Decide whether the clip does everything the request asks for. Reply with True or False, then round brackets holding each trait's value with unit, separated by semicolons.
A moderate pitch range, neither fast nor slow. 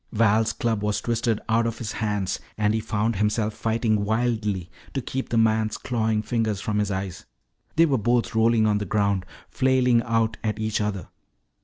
False (1.7 semitones; 180 wpm)